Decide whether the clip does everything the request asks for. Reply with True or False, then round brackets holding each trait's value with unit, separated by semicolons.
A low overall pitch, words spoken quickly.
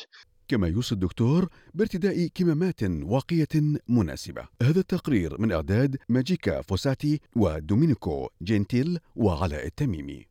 False (125 Hz; 100 wpm)